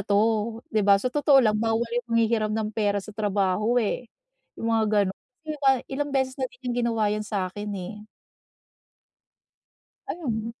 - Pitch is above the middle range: Yes, high, 220 Hz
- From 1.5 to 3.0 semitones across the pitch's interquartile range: Yes, narrow, 2.5 semitones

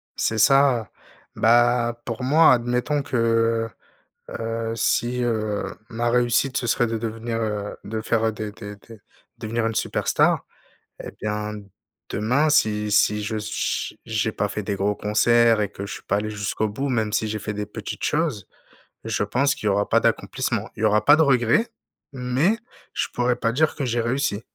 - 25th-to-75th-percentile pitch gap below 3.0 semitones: Yes, narrow, 2.5 semitones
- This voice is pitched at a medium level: No, low, 115 Hz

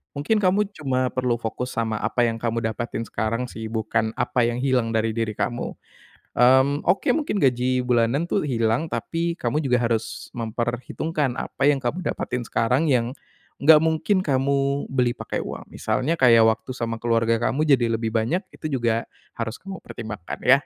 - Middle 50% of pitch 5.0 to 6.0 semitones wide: No, average, 3.5 semitones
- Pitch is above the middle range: No, low, 125 Hz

